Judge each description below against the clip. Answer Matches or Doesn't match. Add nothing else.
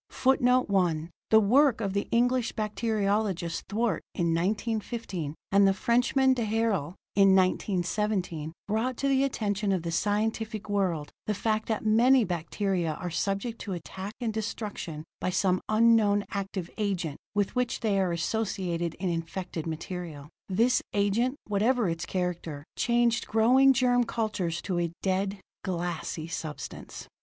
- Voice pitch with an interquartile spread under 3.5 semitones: Doesn't match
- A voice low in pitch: Doesn't match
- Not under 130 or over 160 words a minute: Matches